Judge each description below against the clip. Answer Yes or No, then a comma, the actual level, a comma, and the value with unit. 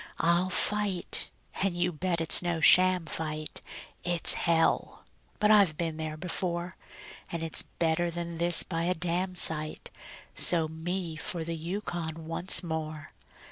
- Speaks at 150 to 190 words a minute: No, average, 140 wpm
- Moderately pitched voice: Yes, medium, 170 Hz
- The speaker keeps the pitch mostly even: Yes, narrow, 1.9 semitones